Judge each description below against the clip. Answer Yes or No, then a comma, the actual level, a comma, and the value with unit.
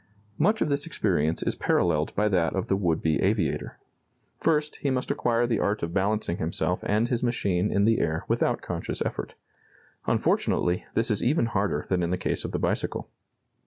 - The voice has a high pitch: No, low, 100 Hz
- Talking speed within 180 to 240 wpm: Yes, average, 190 wpm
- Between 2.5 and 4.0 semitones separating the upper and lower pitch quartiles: No, average, 5.1 semitones